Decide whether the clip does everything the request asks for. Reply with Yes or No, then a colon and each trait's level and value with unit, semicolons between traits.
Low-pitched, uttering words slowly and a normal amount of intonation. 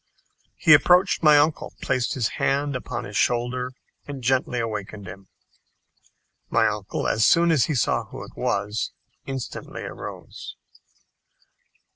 Yes: low, 130 Hz; slow, 130 wpm; average, 4.6 semitones